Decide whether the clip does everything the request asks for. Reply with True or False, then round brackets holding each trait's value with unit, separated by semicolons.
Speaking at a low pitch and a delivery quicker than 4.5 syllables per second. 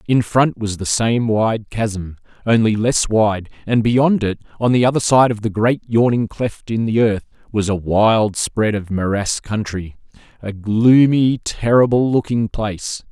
False (110 Hz; 4.1 syllables/s)